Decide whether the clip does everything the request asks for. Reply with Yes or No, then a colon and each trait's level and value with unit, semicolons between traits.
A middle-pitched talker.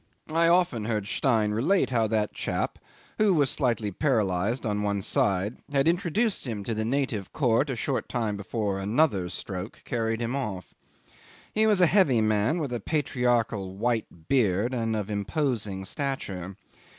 No: low, 115 Hz